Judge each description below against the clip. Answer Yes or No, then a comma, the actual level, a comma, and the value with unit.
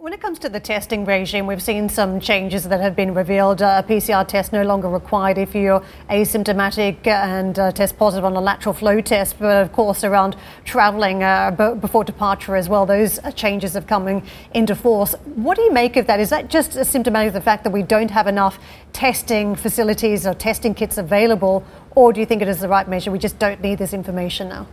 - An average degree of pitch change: No, narrow, 2.0 semitones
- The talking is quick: Yes, fast, 220 wpm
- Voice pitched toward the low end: No, high, 205 Hz